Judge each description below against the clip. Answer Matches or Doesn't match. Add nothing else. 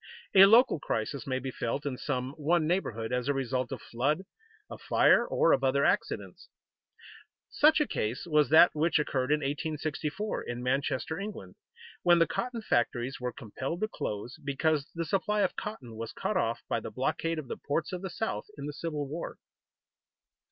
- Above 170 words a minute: Matches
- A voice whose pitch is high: Doesn't match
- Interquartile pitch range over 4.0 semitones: Matches